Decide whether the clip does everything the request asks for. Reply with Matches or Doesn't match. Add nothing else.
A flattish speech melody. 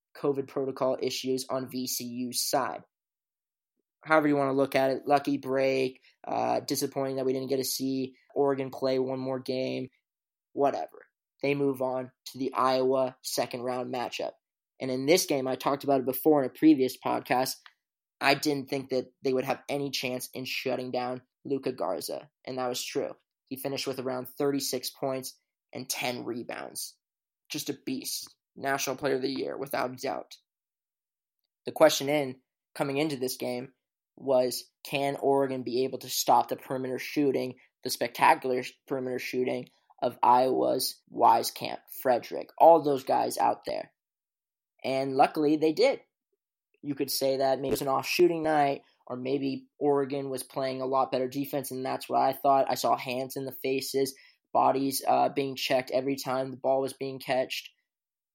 Matches